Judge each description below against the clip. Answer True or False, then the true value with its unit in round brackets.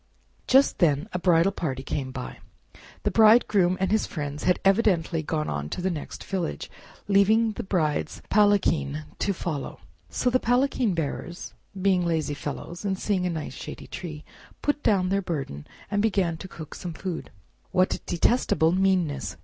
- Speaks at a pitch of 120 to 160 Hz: False (180 Hz)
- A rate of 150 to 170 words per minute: True (160 wpm)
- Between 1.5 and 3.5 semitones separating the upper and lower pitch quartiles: False (4.4 semitones)